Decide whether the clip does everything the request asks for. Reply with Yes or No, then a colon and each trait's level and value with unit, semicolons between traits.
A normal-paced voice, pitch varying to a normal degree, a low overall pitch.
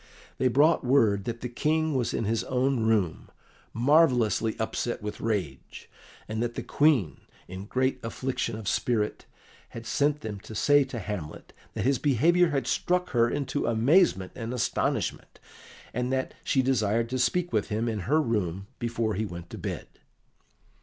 Yes: average, 165 wpm; average, 3.9 semitones; low, 120 Hz